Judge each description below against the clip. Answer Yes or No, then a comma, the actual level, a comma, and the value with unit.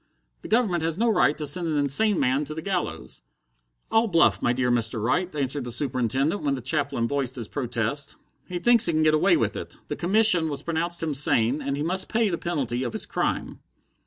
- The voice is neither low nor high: Yes, medium, 150 Hz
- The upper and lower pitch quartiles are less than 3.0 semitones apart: No, average, 5.2 semitones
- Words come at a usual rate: No, fast, 220 wpm